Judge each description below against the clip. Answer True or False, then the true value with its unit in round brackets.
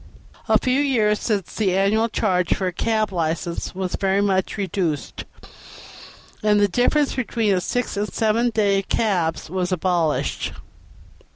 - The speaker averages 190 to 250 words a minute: False (150 wpm)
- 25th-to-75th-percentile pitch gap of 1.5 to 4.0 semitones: True (3.2 semitones)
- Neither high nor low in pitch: False (200 Hz)